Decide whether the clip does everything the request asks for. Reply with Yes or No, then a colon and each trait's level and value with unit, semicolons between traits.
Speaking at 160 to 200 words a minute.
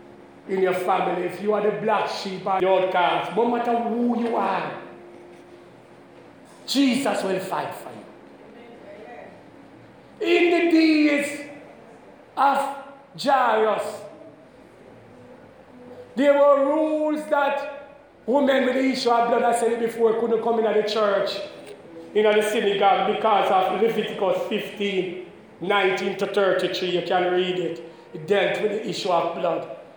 No: average, 140 wpm